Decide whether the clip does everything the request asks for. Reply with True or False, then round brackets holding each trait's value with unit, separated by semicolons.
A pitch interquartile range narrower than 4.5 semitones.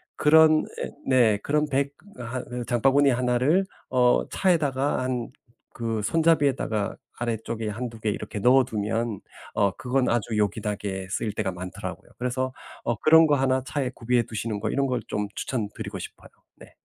True (3.7 semitones)